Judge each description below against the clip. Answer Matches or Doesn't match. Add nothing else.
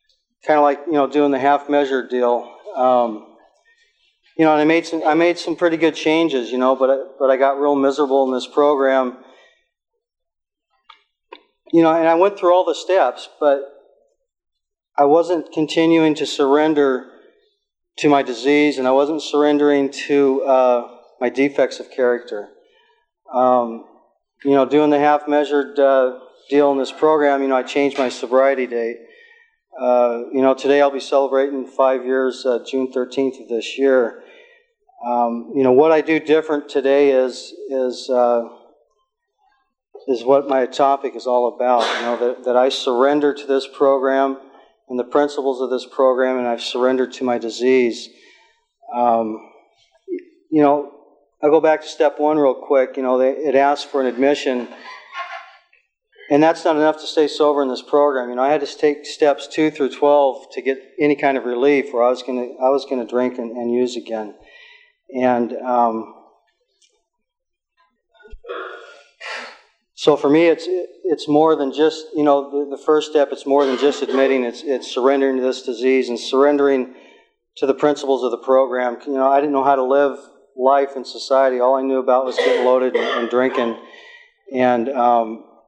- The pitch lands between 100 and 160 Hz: Matches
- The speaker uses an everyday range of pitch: Matches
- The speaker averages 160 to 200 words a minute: Matches